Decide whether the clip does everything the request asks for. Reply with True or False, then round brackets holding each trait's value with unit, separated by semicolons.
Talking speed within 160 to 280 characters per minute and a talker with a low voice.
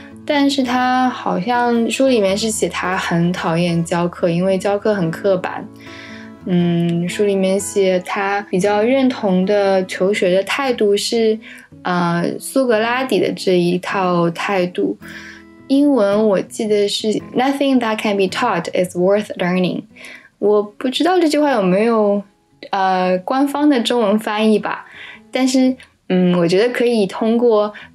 False (265 characters per minute; 205 Hz)